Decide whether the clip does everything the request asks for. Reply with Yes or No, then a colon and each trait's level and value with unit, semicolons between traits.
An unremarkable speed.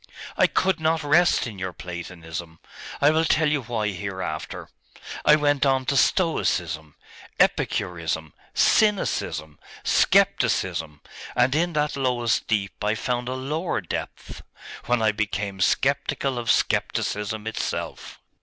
No: slow, 125 wpm